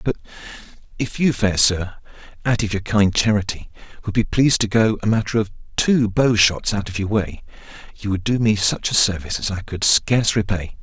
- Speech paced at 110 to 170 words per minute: No, fast, 205 wpm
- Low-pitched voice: Yes, low, 105 Hz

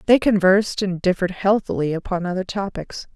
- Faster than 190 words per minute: No, average, 150 wpm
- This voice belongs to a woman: Yes, female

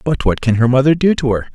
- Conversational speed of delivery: No, fast, 310 wpm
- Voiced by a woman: No, male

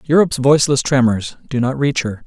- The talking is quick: No, average, 185 wpm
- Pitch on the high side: No, low, 130 Hz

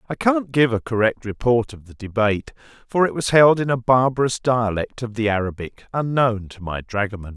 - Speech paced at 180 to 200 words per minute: Yes, average, 195 wpm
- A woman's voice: No, male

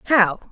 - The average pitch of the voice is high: Yes, high, 210 Hz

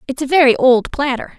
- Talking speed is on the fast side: Yes, fast, 215 wpm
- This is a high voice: Yes, very high, 270 Hz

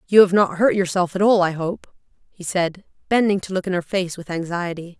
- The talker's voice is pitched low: No, medium, 185 Hz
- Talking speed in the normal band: No, fast, 230 wpm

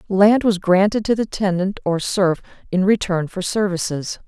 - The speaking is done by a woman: Yes, female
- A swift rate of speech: No, average, 170 wpm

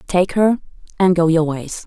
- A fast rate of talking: No, average, 195 wpm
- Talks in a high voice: No, medium, 175 Hz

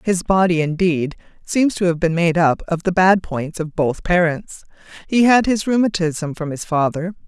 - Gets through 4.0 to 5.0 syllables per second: Yes, 4.6 syllables/s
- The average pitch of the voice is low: No, medium, 175 Hz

